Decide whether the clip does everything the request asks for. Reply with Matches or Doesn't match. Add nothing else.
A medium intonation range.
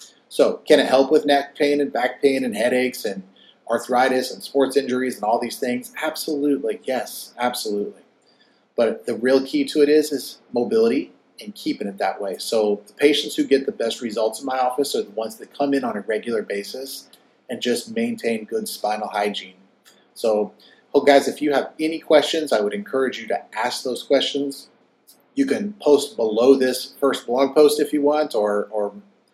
Matches